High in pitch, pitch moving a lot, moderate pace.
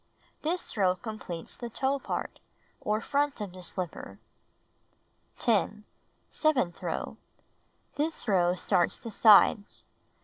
No: high, 215 Hz; wide, 6.3 semitones; slow, 110 wpm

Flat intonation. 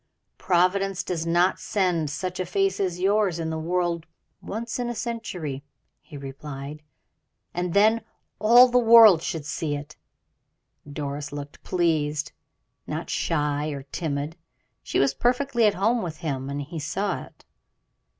No: average, 5.3 semitones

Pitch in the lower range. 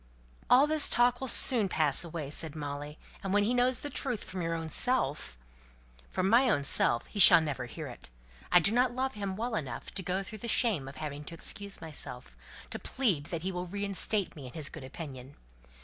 No: medium, 175 Hz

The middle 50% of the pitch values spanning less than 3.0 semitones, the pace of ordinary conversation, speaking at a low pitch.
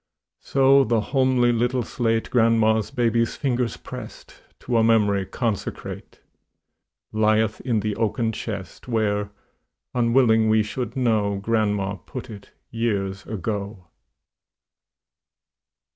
No: narrow, 2.5 semitones; slow, 105 wpm; low, 110 Hz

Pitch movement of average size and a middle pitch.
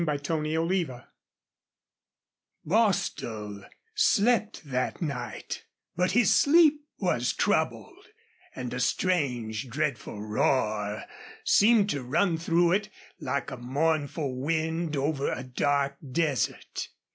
No: wide, 5.8 semitones; medium, 150 Hz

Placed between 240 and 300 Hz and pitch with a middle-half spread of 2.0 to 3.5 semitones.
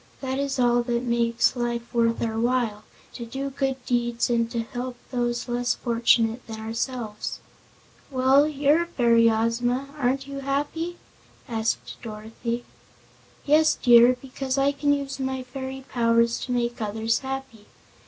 Yes: high, 245 Hz; narrow, 2.5 semitones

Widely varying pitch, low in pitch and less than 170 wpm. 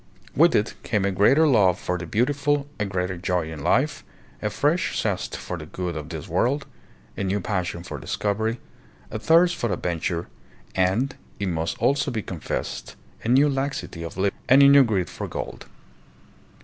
No: wide, 7.2 semitones; low, 105 Hz; average, 175 wpm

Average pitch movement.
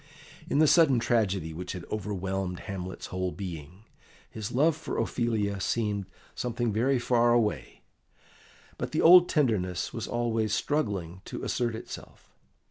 Yes: average, 4.3 semitones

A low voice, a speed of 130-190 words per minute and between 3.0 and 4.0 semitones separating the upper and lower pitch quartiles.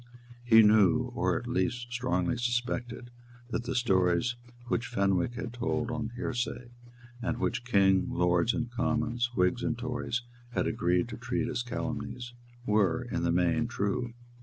Yes: low, 120 Hz; average, 150 wpm; average, 3.7 semitones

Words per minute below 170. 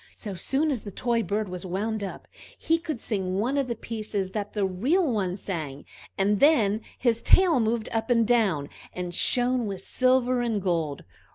No: average, 185 wpm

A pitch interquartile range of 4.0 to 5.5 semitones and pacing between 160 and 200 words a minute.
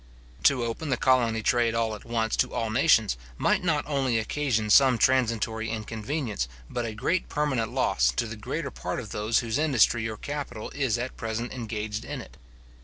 No: average, 3.0 semitones; average, 180 wpm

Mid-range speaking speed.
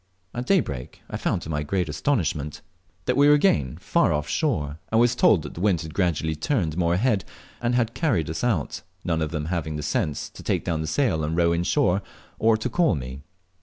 No: fast, 220 wpm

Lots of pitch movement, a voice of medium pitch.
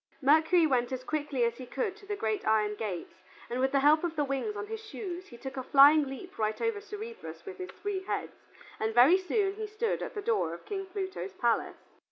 No: wide, 8.3 semitones; very high, 310 Hz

